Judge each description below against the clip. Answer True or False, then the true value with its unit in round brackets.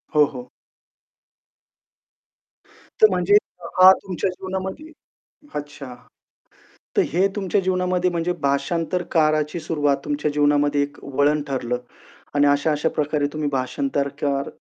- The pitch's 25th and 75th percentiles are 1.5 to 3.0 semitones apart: False (4.1 semitones)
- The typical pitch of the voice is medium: True (150 Hz)